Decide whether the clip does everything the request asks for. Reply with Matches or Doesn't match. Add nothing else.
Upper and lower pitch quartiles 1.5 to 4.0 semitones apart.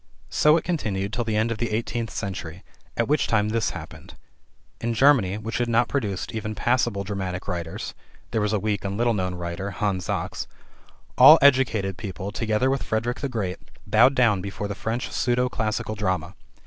Matches